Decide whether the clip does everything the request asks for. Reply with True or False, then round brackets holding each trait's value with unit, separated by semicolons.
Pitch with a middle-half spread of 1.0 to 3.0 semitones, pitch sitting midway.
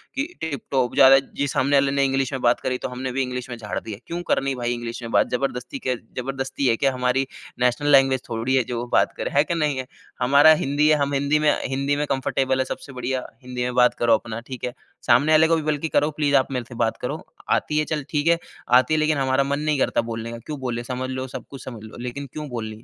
False (2.4 semitones; 130 Hz)